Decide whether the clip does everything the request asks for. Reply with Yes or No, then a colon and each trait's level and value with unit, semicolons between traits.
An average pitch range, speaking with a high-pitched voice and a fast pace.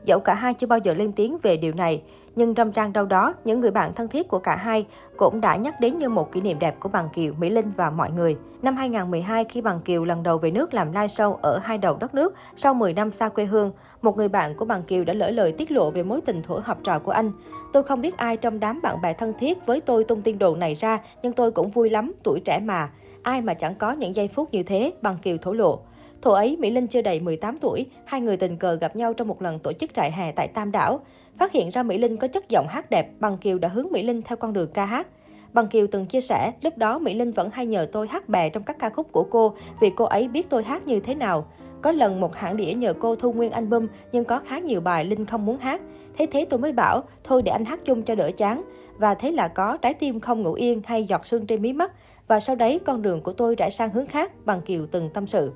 Yes: average, 4.2 semitones; high, 225 Hz; fast, 280 wpm